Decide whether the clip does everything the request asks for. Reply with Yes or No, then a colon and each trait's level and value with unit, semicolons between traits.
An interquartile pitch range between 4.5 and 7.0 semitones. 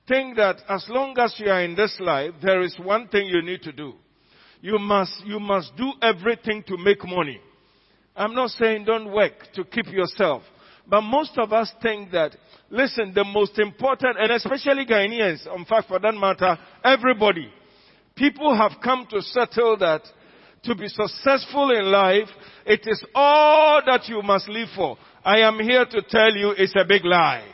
No: average, 3.2 semitones